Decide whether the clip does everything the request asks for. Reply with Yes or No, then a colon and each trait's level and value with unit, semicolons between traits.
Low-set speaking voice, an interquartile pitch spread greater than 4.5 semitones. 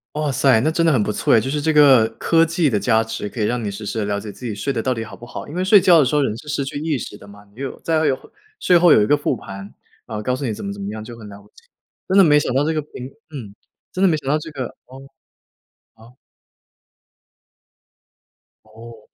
Yes: low, 130 Hz; wide, 5.6 semitones